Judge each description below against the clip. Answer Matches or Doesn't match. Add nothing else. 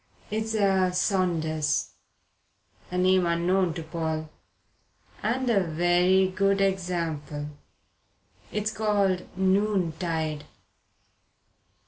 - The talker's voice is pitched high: Doesn't match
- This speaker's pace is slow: Matches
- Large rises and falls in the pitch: Doesn't match